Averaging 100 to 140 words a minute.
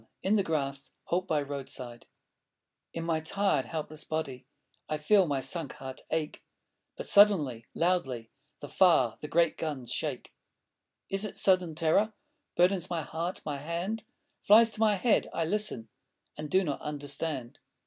No: average, 150 wpm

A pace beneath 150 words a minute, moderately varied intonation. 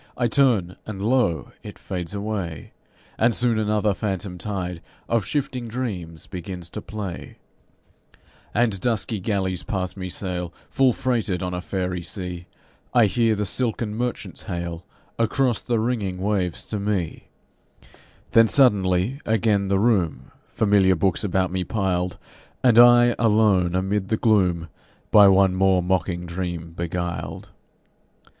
Yes: slow, 135 wpm; average, 3.7 semitones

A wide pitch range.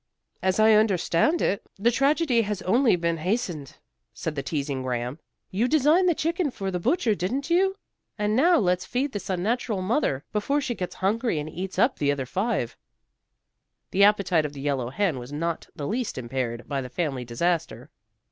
Yes: wide, 8.4 semitones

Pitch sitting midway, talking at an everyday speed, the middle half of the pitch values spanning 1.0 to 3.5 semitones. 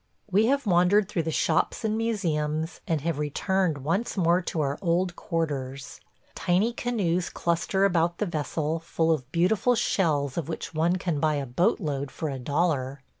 No: medium, 170 Hz; average, 175 wpm; average, 3.9 semitones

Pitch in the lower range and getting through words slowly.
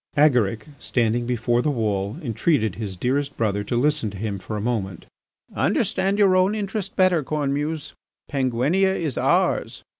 No: low, 125 Hz; average, 150 wpm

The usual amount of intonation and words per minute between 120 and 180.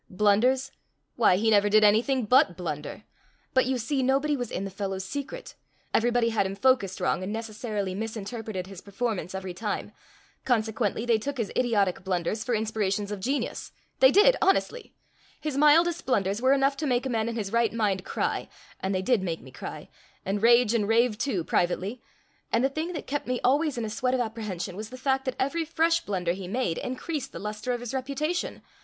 No: average, 4.8 semitones; average, 190 wpm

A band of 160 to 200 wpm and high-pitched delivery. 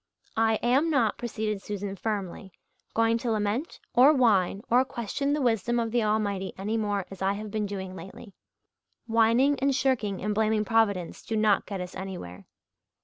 Yes: average, 170 wpm; high, 215 Hz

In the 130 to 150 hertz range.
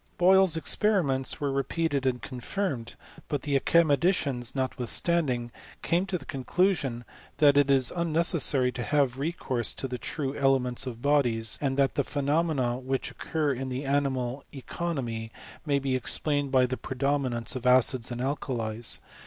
Yes: low, 135 Hz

